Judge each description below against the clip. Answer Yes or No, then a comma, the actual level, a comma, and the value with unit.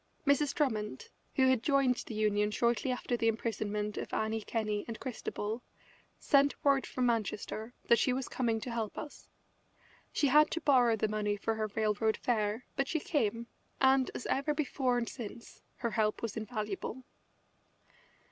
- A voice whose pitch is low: No, high, 235 Hz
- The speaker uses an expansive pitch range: No, average, 3.5 semitones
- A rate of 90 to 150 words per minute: No, average, 165 wpm